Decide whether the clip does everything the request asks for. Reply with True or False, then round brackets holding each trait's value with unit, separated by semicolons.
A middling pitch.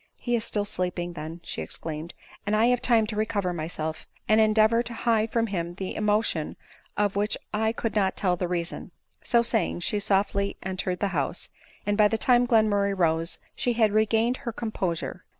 False (205 Hz)